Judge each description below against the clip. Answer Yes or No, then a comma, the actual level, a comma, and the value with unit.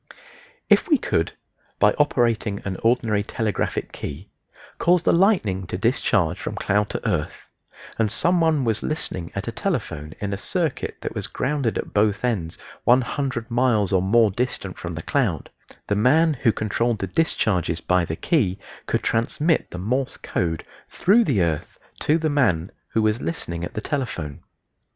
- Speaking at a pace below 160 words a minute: No, average, 165 wpm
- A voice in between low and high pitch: No, low, 110 Hz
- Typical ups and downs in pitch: No, wide, 6.3 semitones